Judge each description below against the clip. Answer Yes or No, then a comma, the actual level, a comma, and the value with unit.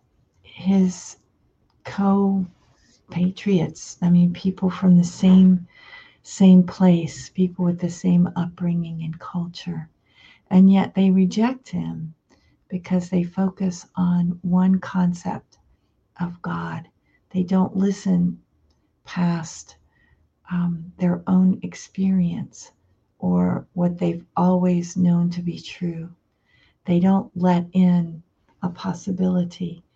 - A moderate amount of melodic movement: No, narrow, 1.3 semitones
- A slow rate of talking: Yes, slow, 105 wpm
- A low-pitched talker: No, medium, 180 Hz